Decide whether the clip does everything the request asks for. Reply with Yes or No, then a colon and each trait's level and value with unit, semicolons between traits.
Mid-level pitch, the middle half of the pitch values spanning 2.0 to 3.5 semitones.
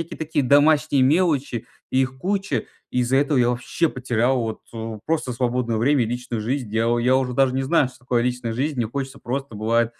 No: low, 130 Hz; average, 3.0 semitones